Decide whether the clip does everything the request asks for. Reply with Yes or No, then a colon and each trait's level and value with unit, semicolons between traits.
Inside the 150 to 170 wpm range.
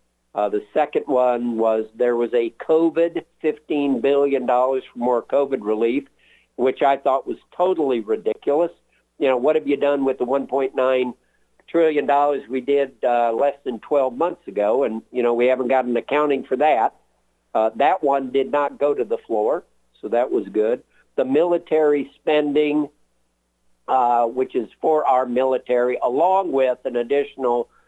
Yes: average, 160 wpm